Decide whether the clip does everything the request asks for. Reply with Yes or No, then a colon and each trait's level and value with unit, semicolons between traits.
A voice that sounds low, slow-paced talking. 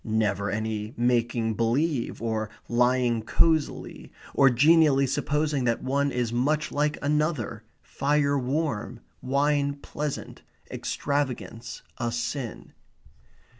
Yes: low, 130 Hz; slow, 100 wpm